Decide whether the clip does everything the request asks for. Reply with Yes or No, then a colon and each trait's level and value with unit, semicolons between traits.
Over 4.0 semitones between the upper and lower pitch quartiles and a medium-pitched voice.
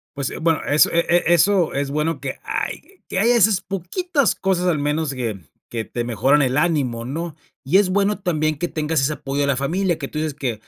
Yes: average, 4.6 semitones; medium, 155 Hz